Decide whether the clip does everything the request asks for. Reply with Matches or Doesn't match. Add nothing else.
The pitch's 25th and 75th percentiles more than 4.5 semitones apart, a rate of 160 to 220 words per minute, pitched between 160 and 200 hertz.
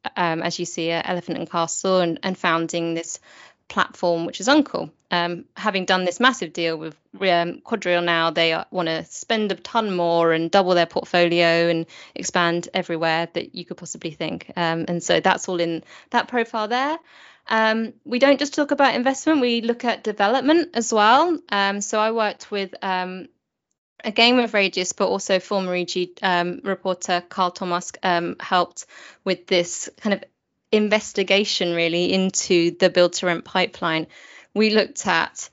Doesn't match